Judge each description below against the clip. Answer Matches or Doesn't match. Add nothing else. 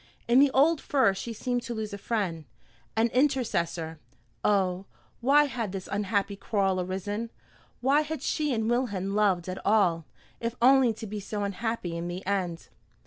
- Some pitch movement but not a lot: Matches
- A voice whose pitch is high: Matches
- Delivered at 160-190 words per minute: Matches